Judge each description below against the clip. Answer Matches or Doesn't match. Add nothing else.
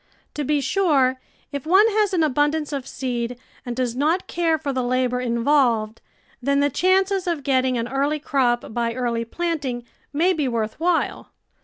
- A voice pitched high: Matches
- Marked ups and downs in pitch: Doesn't match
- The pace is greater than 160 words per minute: Matches